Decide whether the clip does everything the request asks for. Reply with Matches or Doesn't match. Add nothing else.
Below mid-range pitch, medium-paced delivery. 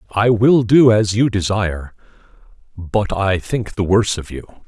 Matches